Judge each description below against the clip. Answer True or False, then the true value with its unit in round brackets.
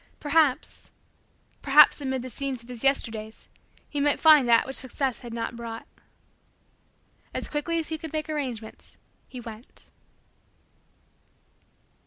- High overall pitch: True (265 Hz)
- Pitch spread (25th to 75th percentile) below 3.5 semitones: False (4.0 semitones)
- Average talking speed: False (130 wpm)